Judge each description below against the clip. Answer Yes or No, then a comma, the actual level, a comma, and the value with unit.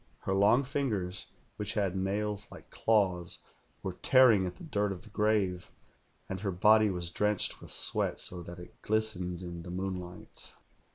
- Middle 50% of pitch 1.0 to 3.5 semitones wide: Yes, average, 3.0 semitones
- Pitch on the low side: Yes, very low, 95 Hz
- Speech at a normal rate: Yes, average, 165 wpm